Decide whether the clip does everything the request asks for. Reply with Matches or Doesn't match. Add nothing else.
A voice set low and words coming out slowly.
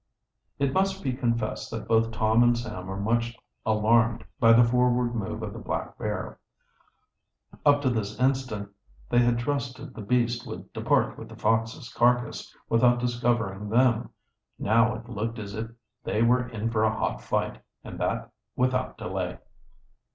Doesn't match